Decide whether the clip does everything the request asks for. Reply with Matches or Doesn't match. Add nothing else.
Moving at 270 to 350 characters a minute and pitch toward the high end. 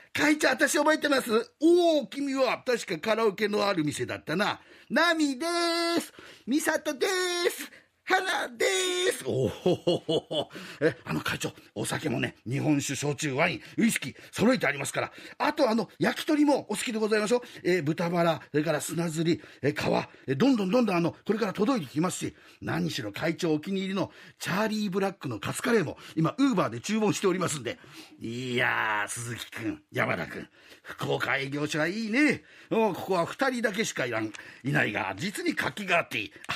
Doesn't match